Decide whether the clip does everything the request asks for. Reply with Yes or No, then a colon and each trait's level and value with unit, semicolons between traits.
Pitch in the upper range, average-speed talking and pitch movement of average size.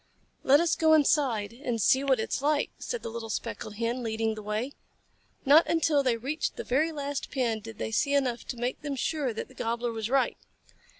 No: very high, 255 Hz; fast, 215 wpm; average, 4.0 semitones